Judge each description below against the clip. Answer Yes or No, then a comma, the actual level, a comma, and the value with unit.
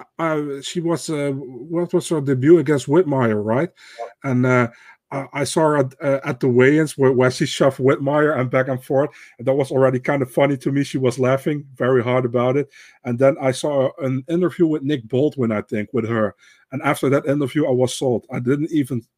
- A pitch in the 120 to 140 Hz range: Yes, low, 135 Hz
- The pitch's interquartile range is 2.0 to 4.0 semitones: Yes, average, 2.8 semitones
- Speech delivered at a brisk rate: Yes, fast, 220 wpm